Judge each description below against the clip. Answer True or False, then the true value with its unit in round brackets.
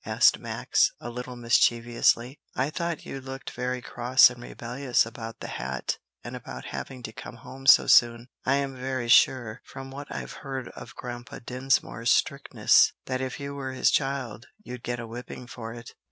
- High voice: False (125 Hz)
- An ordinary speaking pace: True (175 wpm)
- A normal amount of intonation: False (2.0 semitones)